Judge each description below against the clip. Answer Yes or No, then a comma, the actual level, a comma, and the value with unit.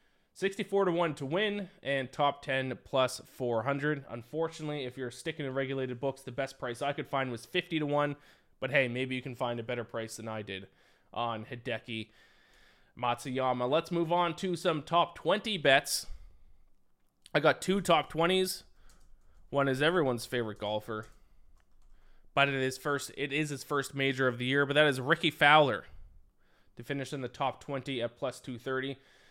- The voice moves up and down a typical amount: Yes, average, 4.1 semitones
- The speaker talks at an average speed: Yes, average, 175 wpm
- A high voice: No, low, 135 Hz